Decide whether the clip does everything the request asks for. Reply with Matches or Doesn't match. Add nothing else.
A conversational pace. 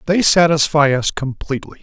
Doesn't match